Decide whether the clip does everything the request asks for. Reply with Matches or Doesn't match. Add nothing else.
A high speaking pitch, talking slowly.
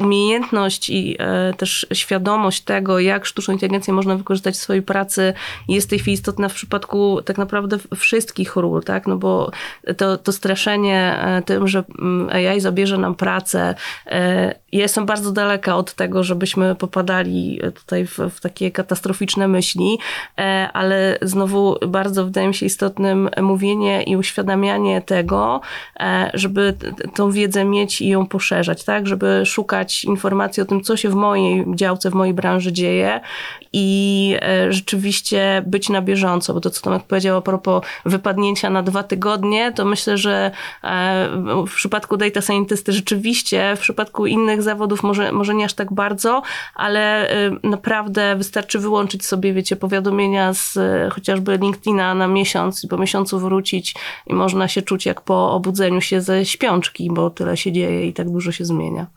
Doesn't match